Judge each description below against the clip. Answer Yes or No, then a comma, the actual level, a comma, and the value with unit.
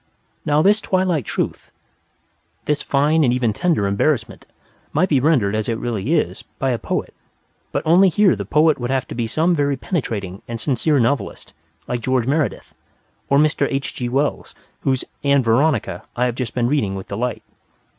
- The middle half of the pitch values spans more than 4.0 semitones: Yes, average, 4.5 semitones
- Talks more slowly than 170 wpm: No, average, 175 wpm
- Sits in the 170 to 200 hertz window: No, low, 135 Hz